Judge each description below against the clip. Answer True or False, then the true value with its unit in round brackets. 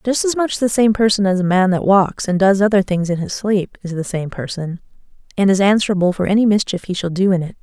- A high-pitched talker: True (195 Hz)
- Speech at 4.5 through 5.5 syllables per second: False (5.9 syllables/s)